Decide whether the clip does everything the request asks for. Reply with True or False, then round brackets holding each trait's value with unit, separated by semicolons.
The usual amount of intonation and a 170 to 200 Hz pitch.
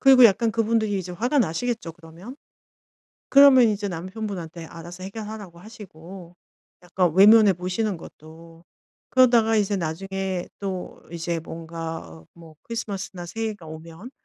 True (4.6 semitones; 190 Hz)